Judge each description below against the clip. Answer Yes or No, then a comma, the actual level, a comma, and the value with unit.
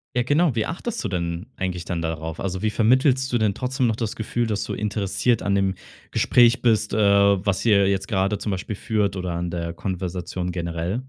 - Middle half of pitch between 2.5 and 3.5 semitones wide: No, average, 3.9 semitones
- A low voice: Yes, low, 100 Hz